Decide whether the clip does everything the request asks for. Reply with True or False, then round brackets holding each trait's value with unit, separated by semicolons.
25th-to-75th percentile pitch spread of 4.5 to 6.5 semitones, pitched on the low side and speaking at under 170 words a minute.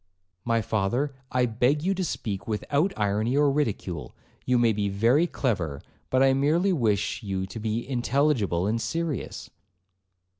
True (5.4 semitones; 120 Hz; 150 wpm)